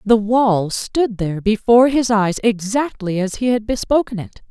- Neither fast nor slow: Yes, average, 175 wpm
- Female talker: Yes, female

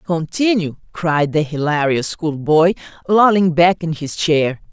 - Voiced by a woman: Yes, female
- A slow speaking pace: Yes, slow, 125 wpm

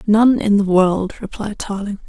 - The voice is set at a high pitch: Yes, high, 205 Hz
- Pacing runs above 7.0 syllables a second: No, 4.4 syllables/s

